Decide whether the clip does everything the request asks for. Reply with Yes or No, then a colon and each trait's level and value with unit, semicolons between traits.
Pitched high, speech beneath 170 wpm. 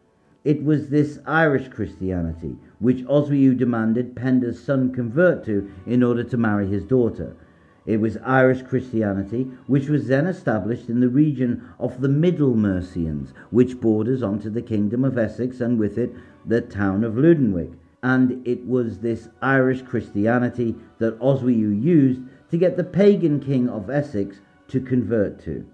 No: low, 125 Hz; average, 155 wpm